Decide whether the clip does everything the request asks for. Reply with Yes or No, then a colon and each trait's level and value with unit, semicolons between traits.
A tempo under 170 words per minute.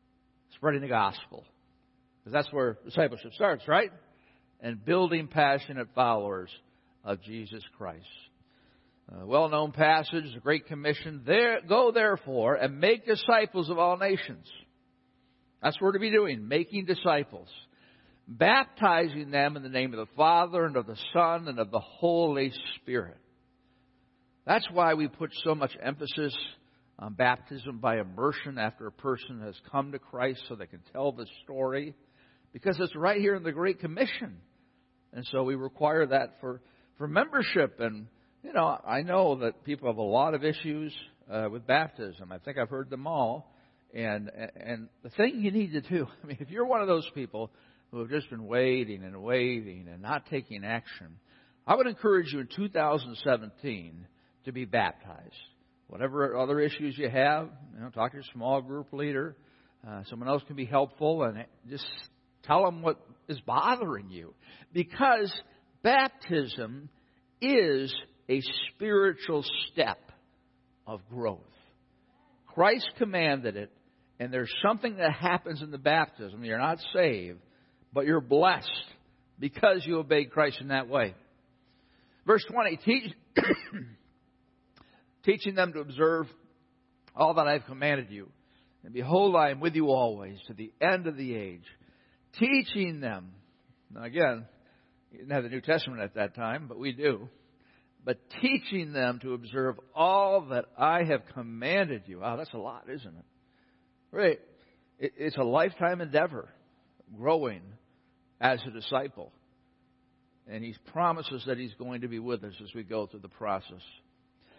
Yes: average, 155 wpm